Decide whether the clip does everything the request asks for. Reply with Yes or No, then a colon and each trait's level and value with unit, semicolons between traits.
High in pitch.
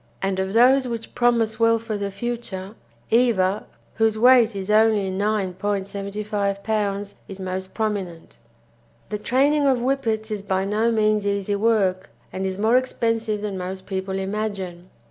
Yes: high, 210 Hz